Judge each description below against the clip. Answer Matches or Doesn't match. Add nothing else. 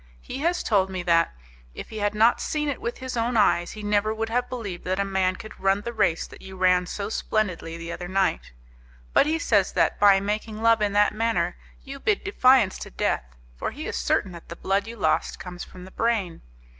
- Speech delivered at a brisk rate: Matches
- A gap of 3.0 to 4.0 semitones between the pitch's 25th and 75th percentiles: Matches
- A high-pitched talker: Matches